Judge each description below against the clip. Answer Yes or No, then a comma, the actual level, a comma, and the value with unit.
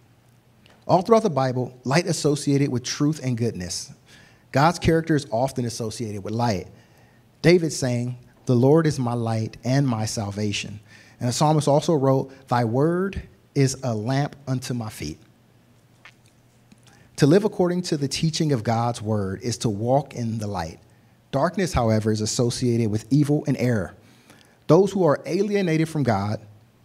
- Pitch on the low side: Yes, low, 125 Hz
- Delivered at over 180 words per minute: No, average, 155 wpm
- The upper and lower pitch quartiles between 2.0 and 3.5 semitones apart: No, average, 4.0 semitones